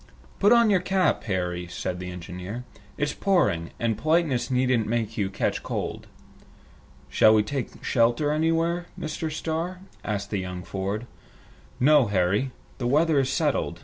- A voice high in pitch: No, low, 120 Hz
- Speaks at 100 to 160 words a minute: Yes, average, 145 wpm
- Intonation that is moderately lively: No, wide, 8.2 semitones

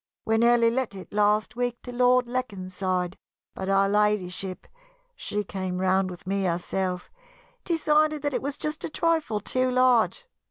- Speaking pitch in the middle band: No, high, 210 Hz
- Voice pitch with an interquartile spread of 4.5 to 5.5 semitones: Yes, average, 5.1 semitones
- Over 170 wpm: No, average, 155 wpm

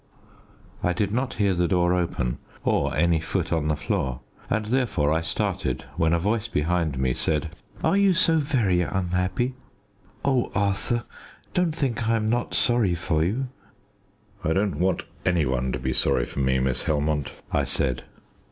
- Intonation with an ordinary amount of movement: No, wide, 6.7 semitones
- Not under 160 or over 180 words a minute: Yes, average, 170 wpm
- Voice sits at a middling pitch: No, very low, 90 Hz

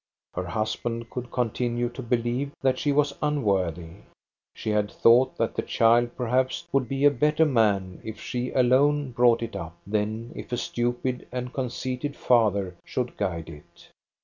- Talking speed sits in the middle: Yes, average, 160 wpm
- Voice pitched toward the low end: Yes, low, 120 Hz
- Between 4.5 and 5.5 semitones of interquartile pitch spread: No, average, 3.3 semitones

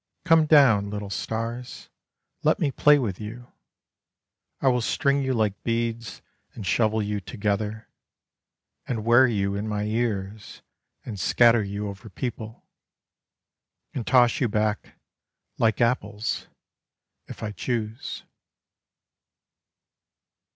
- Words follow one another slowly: Yes, slow, 115 wpm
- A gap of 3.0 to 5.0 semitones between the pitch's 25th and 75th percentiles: No, narrow, 2.6 semitones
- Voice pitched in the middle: No, low, 110 Hz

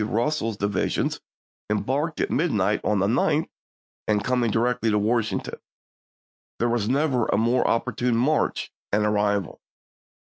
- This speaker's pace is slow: Yes, slow, 130 wpm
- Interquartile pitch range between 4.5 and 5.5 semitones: No, average, 3.2 semitones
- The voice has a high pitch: No, low, 115 Hz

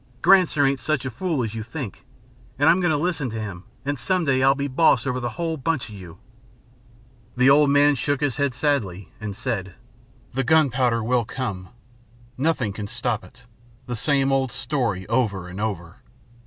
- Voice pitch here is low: Yes, low, 130 Hz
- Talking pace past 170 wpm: Yes, average, 185 wpm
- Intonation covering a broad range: No, average, 4.6 semitones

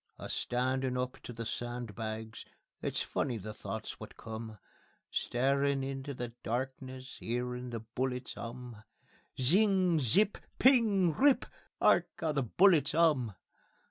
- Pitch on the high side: No, low, 130 Hz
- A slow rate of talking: Yes, slow, 125 wpm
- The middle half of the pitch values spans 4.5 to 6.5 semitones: No, average, 3.7 semitones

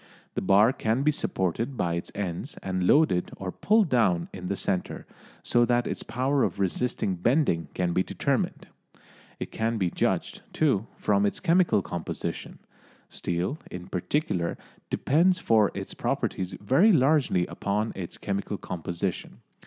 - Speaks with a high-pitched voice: No, low, 100 Hz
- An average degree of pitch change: No, wide, 6.6 semitones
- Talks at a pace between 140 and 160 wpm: Yes, average, 145 wpm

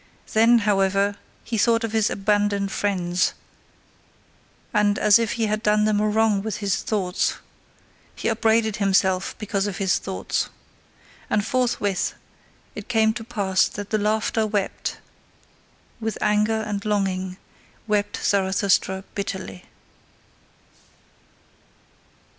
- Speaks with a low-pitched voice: No, high, 205 Hz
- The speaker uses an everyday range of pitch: No, narrow, 1.9 semitones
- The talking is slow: Yes, slow, 120 wpm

